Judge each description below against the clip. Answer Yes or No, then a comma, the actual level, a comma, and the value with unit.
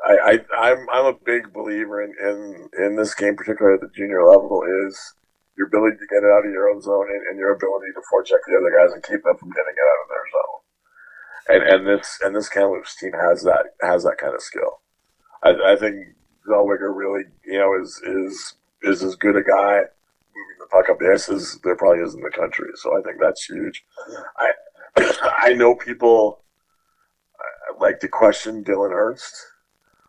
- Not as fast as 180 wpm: No, average, 200 wpm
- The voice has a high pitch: No, low, 115 Hz